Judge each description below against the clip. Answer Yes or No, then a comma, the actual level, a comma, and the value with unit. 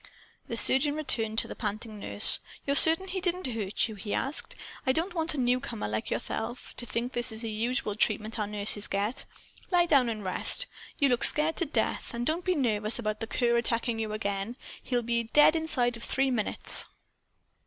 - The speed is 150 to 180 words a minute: No, average, 195 wpm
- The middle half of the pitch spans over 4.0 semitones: Yes, average, 4.7 semitones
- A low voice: No, high, 235 Hz